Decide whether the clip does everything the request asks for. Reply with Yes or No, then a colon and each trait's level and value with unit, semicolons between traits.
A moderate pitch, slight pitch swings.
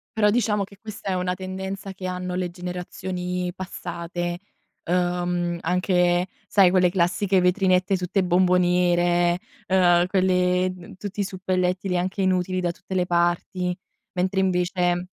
Yes: medium, 180 Hz; narrow, 1.1 semitones